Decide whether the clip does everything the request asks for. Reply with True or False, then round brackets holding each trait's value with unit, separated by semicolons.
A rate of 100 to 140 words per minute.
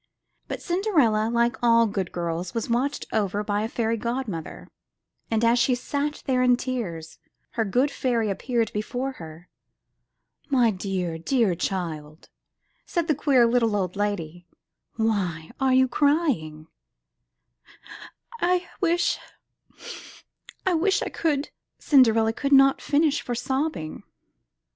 True (135 wpm)